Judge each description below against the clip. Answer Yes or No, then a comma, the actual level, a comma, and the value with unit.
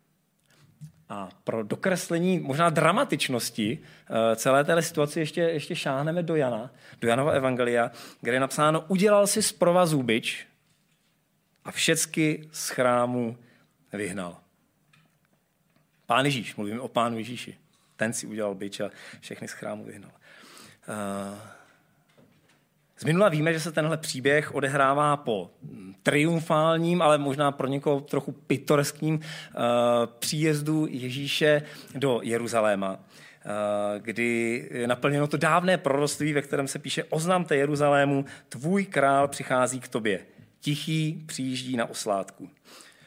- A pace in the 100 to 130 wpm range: Yes, average, 125 wpm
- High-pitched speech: No, medium, 145 Hz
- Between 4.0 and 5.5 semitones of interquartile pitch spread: Yes, average, 4.7 semitones